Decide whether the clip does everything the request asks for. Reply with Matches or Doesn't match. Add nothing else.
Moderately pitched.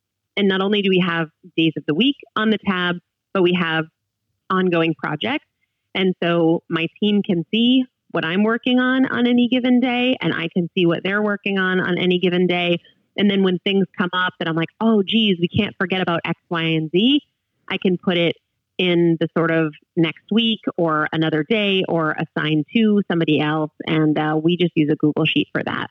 Matches